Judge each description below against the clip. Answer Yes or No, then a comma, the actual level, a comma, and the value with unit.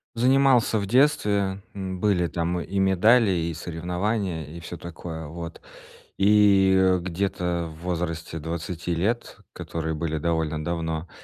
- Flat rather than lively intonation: No, average, 3.1 semitones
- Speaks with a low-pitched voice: Yes, very low, 90 Hz